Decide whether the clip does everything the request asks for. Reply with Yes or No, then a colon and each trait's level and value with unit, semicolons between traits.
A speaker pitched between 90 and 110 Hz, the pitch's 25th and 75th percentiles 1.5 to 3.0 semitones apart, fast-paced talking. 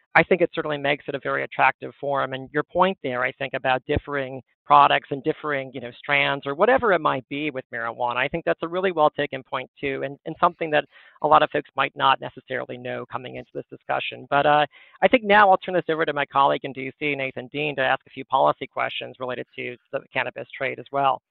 No: medium, 140 Hz; narrow, 2.4 semitones; fast, 240 wpm